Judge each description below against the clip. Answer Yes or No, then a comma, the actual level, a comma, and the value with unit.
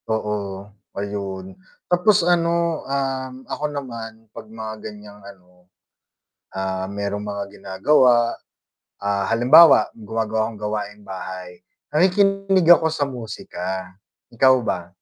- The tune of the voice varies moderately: No, wide, 5.7 semitones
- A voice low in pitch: Yes, low, 110 Hz